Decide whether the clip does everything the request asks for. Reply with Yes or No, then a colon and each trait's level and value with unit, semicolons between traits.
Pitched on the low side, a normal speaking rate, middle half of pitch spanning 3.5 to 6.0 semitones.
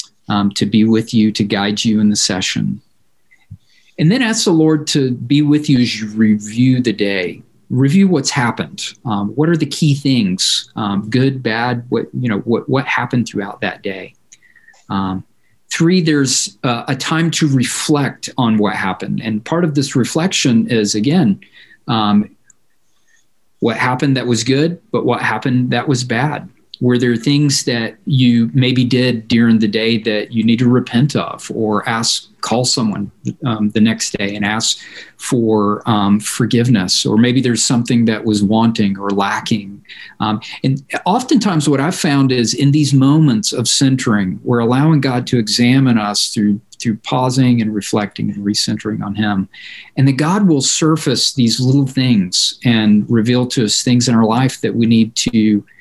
Yes: low, 120 Hz; average, 170 wpm; average, 4.1 semitones